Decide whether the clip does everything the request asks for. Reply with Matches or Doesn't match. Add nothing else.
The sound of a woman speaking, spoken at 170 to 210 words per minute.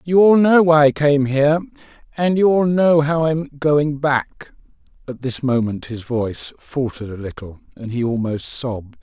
Doesn't match